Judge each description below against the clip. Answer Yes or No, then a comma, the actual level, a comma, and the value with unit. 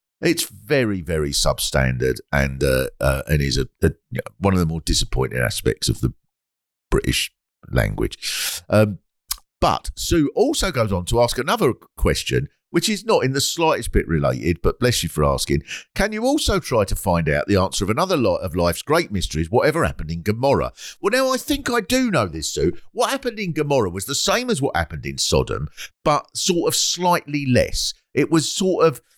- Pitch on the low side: Yes, low, 100 Hz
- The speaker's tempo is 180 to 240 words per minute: Yes, average, 195 wpm